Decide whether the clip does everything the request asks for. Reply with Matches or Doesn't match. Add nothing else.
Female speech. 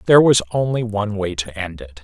Doesn't match